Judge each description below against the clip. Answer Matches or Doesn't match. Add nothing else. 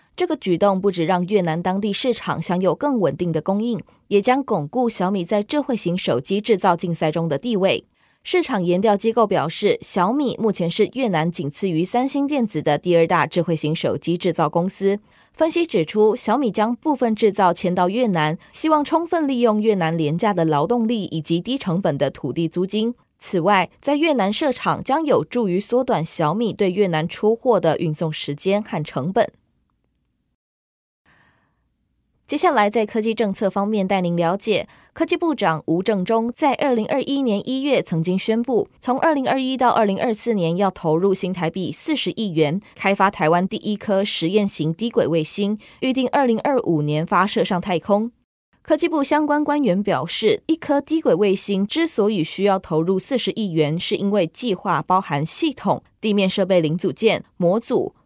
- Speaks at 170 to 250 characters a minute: Doesn't match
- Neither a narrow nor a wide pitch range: Doesn't match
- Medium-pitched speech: Doesn't match